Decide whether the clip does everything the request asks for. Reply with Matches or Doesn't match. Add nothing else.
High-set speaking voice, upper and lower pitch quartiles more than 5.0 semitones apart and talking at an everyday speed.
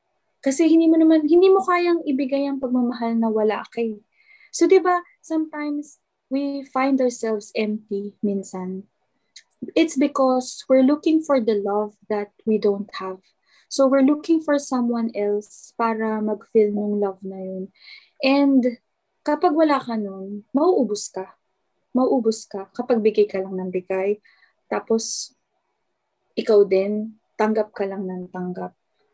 Matches